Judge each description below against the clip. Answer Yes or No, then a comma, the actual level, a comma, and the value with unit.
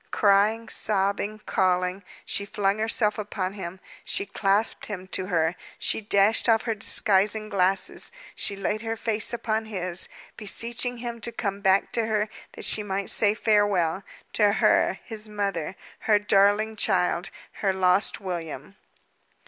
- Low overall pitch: No, high, 205 Hz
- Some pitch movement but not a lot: No, narrow, 2.2 semitones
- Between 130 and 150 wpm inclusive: Yes, average, 145 wpm